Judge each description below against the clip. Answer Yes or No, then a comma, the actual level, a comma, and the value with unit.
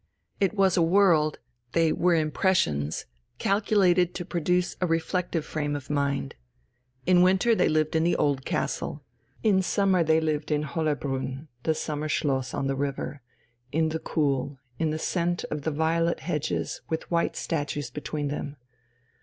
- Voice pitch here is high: No, medium, 160 Hz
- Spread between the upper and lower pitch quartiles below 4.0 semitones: Yes, average, 3.2 semitones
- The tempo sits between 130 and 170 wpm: Yes, average, 155 wpm